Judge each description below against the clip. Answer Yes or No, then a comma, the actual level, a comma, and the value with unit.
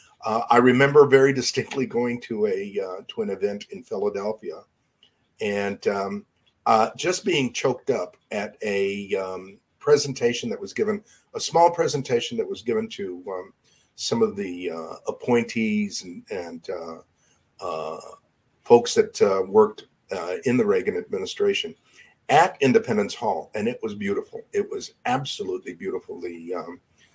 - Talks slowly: No, average, 150 wpm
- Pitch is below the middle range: No, medium, 185 Hz